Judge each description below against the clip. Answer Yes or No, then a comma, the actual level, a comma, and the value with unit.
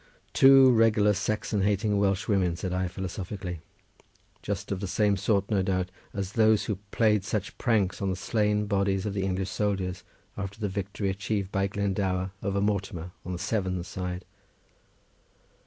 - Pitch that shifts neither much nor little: No, narrow, 1.9 semitones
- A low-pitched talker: Yes, low, 100 Hz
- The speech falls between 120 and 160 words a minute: Yes, average, 155 wpm